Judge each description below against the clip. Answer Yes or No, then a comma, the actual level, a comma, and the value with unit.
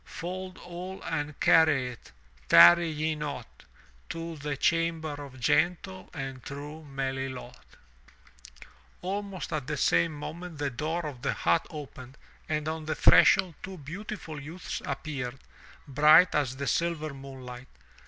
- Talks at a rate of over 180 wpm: No, slow, 135 wpm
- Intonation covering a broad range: No, average, 3.5 semitones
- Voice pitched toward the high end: No, medium, 150 Hz